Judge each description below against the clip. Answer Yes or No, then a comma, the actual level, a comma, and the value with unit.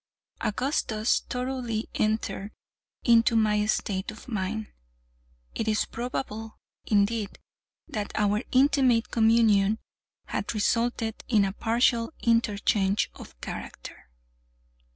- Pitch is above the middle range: Yes, high, 220 Hz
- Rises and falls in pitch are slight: Yes, narrow, 2.0 semitones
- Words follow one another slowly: Yes, slow, 95 wpm